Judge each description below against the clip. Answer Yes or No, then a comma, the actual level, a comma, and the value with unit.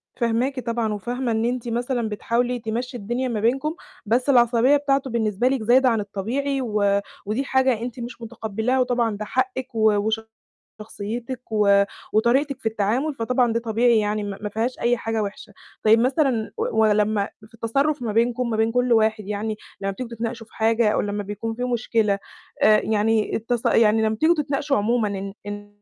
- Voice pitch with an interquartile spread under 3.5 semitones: Yes, average, 2.7 semitones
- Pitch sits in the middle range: No, high, 230 Hz